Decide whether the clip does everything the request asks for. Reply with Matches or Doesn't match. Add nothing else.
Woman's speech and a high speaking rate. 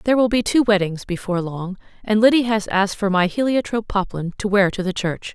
Matches